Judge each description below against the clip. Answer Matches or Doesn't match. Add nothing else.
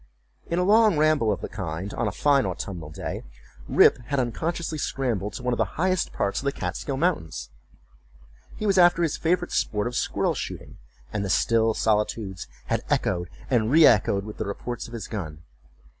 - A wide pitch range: Matches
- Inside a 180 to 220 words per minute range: Matches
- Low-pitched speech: Matches